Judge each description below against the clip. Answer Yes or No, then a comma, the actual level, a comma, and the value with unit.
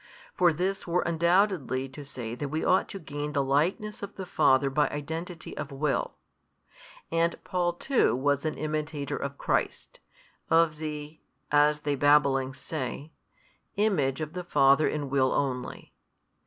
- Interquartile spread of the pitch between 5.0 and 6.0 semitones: No, average, 3.3 semitones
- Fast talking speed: No, average, 150 wpm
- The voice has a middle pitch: Yes, medium, 150 Hz